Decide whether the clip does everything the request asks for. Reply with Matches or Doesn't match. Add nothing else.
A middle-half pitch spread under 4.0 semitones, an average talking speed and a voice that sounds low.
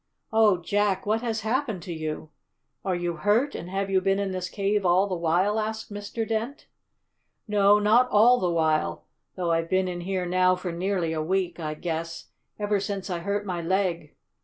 Doesn't match